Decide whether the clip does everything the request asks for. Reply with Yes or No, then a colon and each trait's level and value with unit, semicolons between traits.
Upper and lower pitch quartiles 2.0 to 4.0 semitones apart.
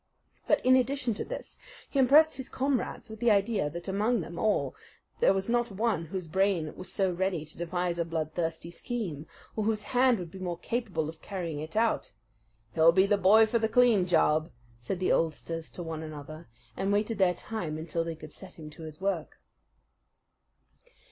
No: average, 5.1 semitones